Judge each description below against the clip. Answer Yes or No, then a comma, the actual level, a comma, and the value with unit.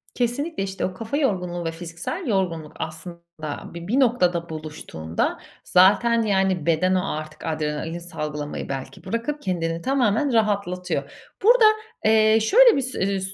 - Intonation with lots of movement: Yes, wide, 5.8 semitones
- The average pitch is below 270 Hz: Yes, medium, 185 Hz